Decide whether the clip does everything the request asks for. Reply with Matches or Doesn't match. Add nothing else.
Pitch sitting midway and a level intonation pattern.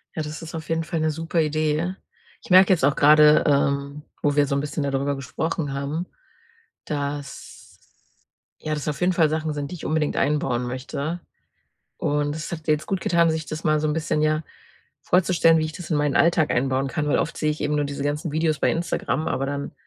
Matches